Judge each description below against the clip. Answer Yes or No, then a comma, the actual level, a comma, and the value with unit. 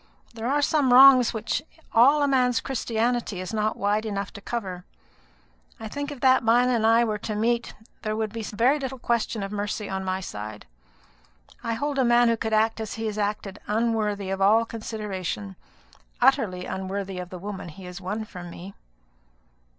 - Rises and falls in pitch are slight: No, average, 3.3 semitones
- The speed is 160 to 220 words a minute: Yes, average, 185 wpm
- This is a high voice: Yes, high, 220 Hz